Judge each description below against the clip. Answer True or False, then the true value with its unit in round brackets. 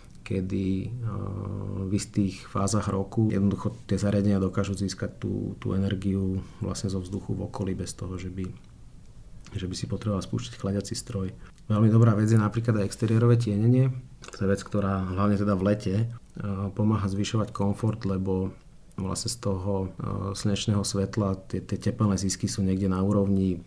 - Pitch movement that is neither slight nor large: False (2.0 semitones)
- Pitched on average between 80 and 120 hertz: True (100 Hz)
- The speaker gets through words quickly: False (155 wpm)